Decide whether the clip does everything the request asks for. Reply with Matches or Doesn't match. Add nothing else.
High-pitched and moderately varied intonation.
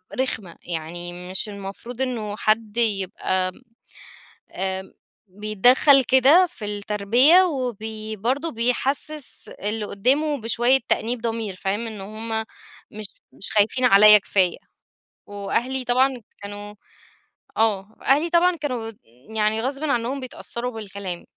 Matches